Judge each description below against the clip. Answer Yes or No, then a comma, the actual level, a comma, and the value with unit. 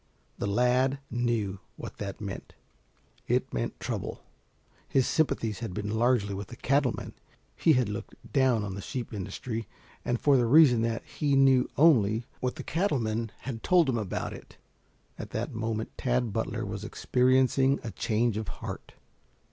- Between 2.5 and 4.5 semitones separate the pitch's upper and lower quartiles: Yes, average, 3.3 semitones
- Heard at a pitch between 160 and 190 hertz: No, low, 120 Hz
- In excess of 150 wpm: Yes, average, 165 wpm